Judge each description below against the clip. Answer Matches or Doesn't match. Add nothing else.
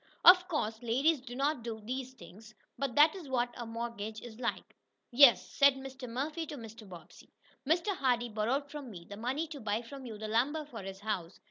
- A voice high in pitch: Matches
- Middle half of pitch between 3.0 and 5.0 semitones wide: Matches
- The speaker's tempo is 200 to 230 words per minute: Matches